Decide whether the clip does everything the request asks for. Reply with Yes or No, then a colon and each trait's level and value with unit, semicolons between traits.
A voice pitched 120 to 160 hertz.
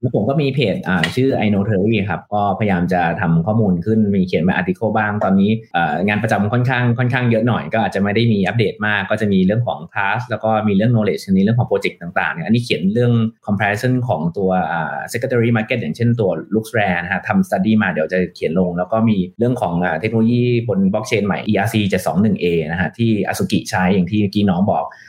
No: low, 105 Hz